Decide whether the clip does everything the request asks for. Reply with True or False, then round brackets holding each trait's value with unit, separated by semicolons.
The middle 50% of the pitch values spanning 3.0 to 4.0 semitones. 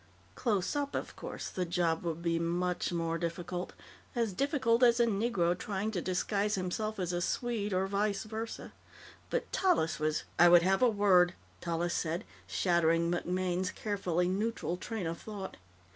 True (3.7 semitones)